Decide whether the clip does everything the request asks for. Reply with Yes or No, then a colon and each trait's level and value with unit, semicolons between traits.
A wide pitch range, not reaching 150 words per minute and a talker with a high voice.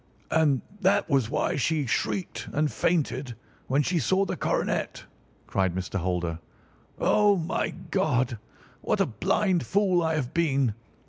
No: wide, 6.8 semitones; average, 140 wpm; medium, 150 Hz